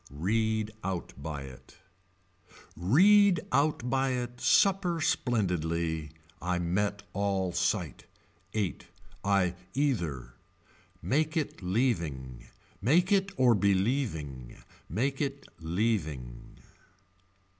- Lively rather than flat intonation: Yes, wide, 8.2 semitones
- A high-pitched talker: No, low, 100 Hz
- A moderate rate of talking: No, slow, 90 wpm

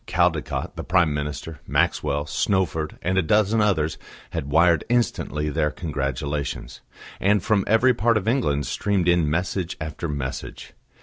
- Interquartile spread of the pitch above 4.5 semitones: Yes, wide, 5.4 semitones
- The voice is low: Yes, very low, 85 Hz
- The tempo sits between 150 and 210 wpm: No, average, 140 wpm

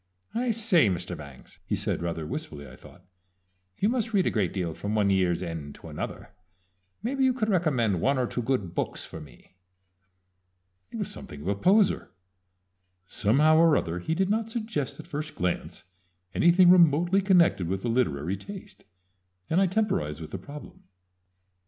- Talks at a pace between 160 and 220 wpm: Yes, average, 170 wpm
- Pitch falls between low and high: No, low, 130 Hz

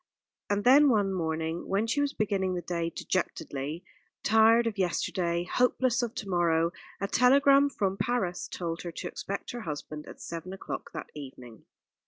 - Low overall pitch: No, high, 190 Hz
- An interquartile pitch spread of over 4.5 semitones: Yes, average, 5.3 semitones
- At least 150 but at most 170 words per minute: Yes, average, 165 wpm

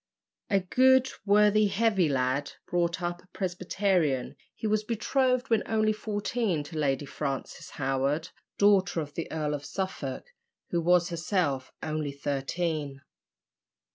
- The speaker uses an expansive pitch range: Yes, wide, 6.2 semitones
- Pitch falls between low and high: Yes, medium, 175 Hz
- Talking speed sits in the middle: No, slow, 130 wpm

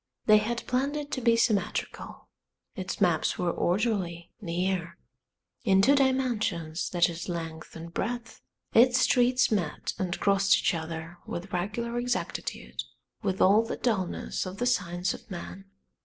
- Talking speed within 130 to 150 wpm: Yes, average, 145 wpm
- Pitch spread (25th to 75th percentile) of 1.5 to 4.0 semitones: No, average, 5.3 semitones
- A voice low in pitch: No, high, 195 Hz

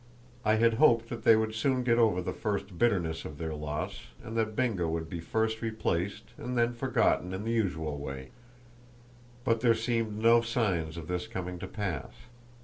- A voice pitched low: Yes, low, 110 Hz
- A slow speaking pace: No, average, 185 wpm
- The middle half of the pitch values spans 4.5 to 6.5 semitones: Yes, average, 5.1 semitones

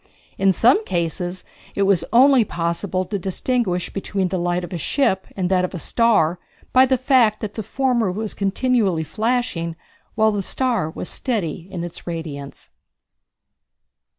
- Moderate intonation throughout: Yes, average, 5.0 semitones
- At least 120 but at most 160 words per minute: Yes, average, 155 wpm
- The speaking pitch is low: No, high, 195 Hz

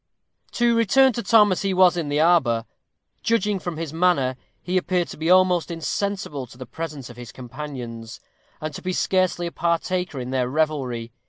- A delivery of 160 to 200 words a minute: Yes, average, 185 wpm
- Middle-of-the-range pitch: Yes, medium, 165 Hz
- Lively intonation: Yes, wide, 5.9 semitones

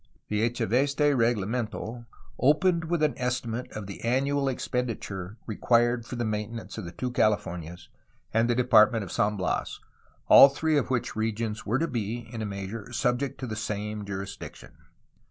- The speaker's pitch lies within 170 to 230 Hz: No, low, 115 Hz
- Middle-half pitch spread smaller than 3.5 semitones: Yes, average, 3.1 semitones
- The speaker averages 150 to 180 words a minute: Yes, average, 160 wpm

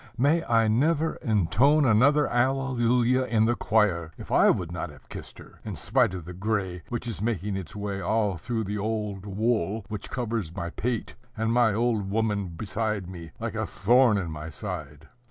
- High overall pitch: No, low, 110 Hz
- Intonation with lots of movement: No, average, 4.2 semitones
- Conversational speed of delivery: Yes, average, 185 wpm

